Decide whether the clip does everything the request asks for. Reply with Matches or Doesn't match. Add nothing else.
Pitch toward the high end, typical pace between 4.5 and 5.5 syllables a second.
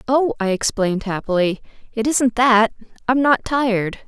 Matches